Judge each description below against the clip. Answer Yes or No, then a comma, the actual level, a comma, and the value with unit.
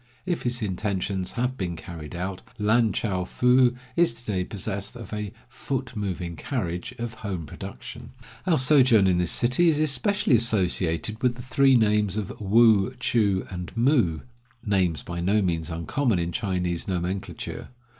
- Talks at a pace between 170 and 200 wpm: No, average, 160 wpm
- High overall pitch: No, low, 105 Hz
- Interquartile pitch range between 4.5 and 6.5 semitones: Yes, average, 5.2 semitones